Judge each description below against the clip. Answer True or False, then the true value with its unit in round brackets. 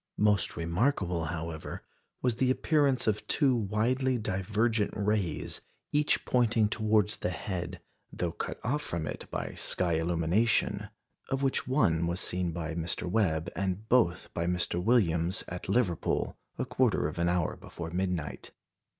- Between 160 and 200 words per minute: False (145 wpm)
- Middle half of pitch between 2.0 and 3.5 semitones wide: False (5.3 semitones)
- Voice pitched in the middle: False (95 Hz)